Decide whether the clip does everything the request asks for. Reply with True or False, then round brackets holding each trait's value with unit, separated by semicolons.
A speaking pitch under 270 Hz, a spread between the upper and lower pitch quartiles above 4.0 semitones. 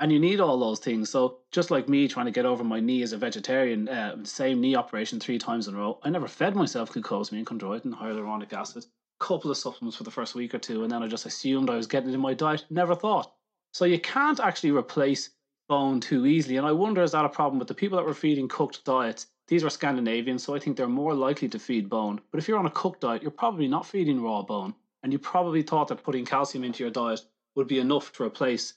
True (135 Hz; 4.7 semitones)